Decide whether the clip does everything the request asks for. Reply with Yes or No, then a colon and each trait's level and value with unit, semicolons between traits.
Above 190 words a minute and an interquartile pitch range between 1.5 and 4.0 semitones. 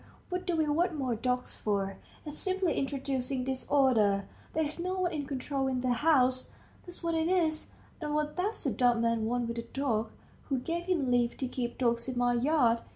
No: average, 200 wpm; average, 4.6 semitones